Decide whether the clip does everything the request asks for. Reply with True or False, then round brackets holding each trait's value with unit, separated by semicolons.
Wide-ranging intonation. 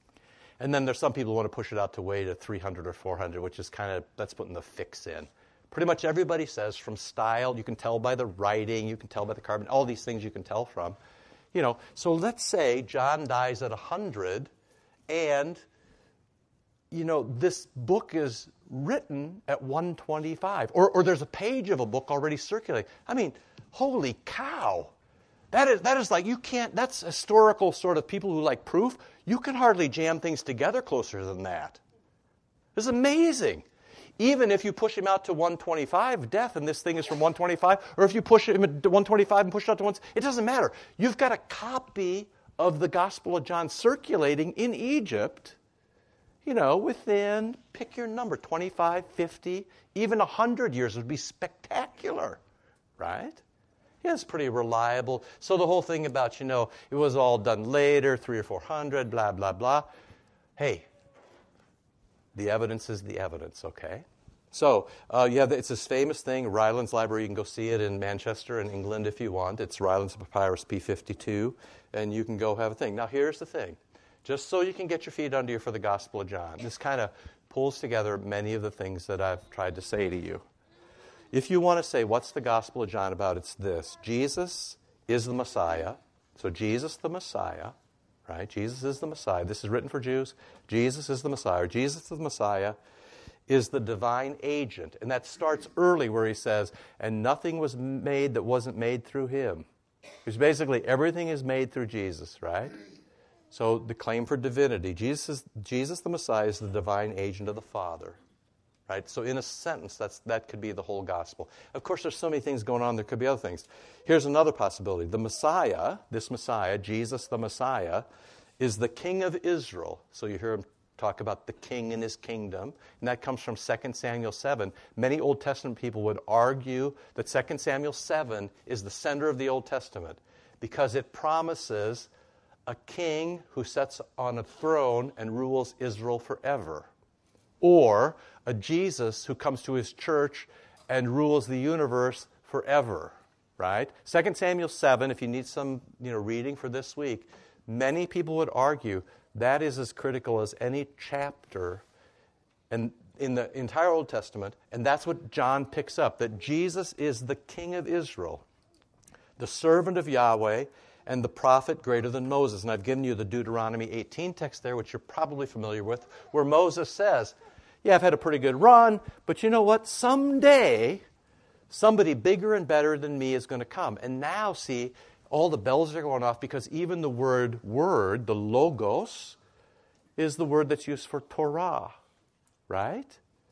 True (6.7 semitones)